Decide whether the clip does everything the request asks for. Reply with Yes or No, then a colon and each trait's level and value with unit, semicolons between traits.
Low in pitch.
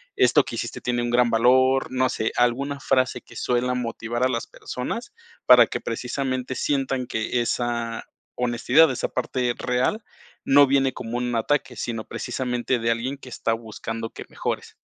Yes: low, 125 Hz